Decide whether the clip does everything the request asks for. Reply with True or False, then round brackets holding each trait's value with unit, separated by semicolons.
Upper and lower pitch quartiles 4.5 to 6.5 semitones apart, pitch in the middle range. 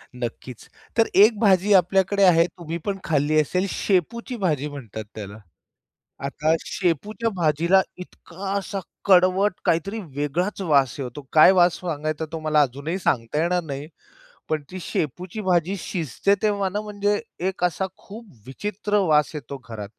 True (4.8 semitones; 175 Hz)